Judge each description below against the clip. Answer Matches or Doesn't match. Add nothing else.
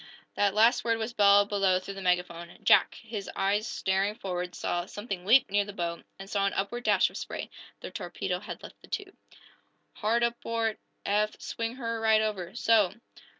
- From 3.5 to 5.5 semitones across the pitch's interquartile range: Doesn't match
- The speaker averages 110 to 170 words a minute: Doesn't match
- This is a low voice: Doesn't match